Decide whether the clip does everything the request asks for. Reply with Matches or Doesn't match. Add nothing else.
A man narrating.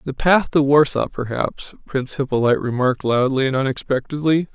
Matches